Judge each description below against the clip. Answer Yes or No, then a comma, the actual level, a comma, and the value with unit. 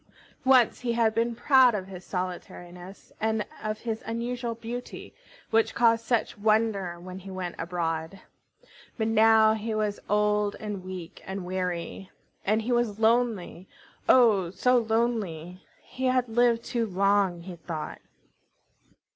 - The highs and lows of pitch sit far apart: No, average, 3.8 semitones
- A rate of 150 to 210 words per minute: No, average, 140 wpm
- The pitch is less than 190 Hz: No, high, 215 Hz